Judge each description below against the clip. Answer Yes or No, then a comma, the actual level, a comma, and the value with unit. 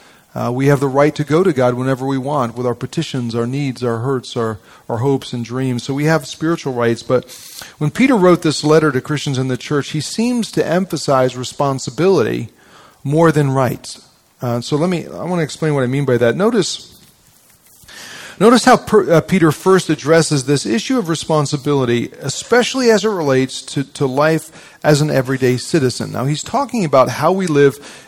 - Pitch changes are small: No, average, 3.8 semitones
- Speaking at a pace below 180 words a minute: No, average, 195 wpm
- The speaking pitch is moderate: Yes, medium, 145 Hz